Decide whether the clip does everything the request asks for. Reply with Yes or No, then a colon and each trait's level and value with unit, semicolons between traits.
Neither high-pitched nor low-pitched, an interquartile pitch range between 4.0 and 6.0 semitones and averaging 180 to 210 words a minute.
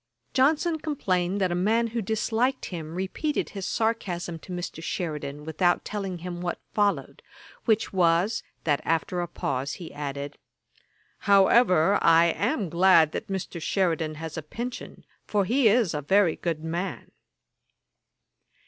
No: medium, 180 Hz; average, 4.3 semitones; average, 145 wpm